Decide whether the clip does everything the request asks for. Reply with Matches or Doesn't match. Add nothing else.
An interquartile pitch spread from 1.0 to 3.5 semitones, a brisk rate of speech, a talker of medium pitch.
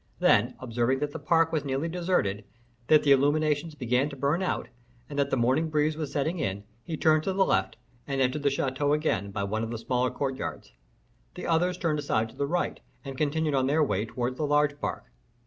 Matches